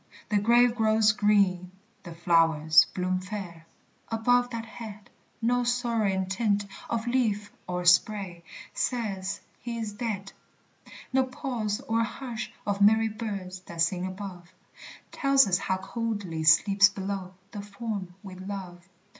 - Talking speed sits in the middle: No, slow, 130 wpm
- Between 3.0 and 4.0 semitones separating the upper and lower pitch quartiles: Yes, average, 3.6 semitones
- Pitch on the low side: No, high, 205 Hz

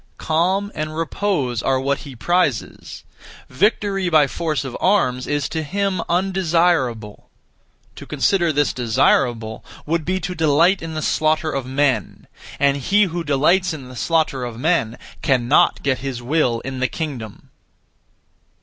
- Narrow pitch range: No, average, 5.1 semitones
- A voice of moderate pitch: Yes, medium, 155 Hz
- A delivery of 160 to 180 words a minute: No, average, 145 wpm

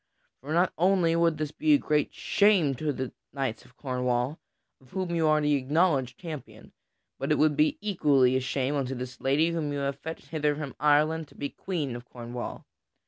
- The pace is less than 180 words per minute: No, average, 195 wpm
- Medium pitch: Yes, medium, 150 Hz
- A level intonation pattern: No, average, 3.7 semitones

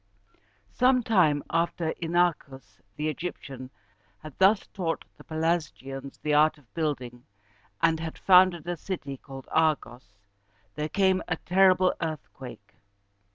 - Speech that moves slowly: Yes, slow, 120 wpm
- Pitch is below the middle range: No, medium, 160 Hz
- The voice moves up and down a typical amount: Yes, average, 4.4 semitones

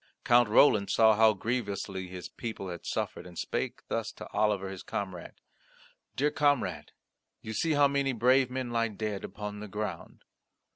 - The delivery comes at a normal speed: Yes, average, 160 wpm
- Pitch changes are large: No, average, 4.3 semitones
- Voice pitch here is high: No, low, 110 Hz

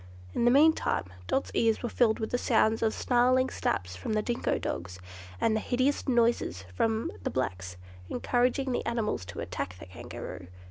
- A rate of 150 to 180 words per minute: Yes, average, 170 wpm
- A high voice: Yes, high, 225 Hz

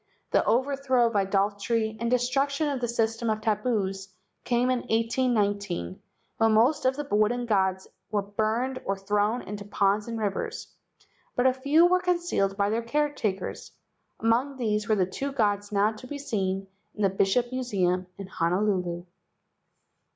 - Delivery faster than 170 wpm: No, average, 160 wpm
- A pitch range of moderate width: Yes, average, 4.0 semitones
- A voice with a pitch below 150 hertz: No, high, 220 Hz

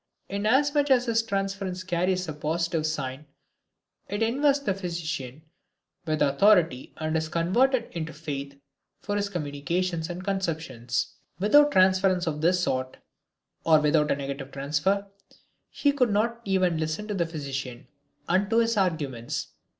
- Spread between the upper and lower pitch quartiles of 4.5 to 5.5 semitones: Yes, average, 5.0 semitones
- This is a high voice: No, medium, 175 Hz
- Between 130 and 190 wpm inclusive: Yes, average, 140 wpm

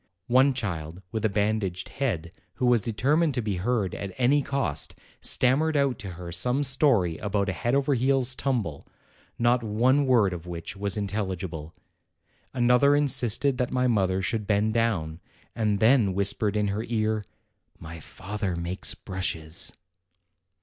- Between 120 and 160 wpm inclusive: Yes, average, 150 wpm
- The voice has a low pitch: Yes, low, 110 Hz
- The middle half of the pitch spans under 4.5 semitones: No, average, 5.1 semitones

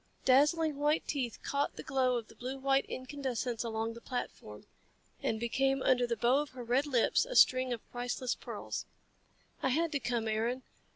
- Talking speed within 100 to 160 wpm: No, average, 180 wpm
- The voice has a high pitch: Yes, very high, 255 Hz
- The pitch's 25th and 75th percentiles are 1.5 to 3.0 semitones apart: Yes, narrow, 2.6 semitones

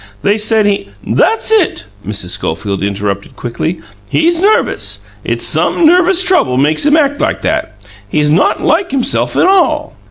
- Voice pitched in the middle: No, high, 210 Hz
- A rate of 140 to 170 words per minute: Yes, average, 160 wpm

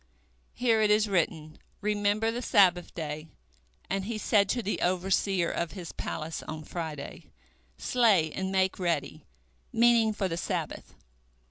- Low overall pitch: No, high, 190 Hz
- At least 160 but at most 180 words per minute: No, average, 140 wpm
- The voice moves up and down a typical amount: Yes, average, 4.0 semitones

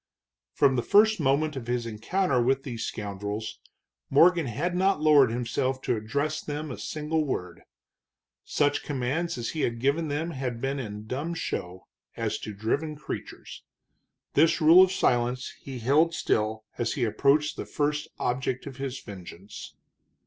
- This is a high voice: No, low, 135 Hz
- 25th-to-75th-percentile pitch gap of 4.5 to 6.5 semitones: Yes, average, 4.8 semitones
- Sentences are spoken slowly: No, average, 155 wpm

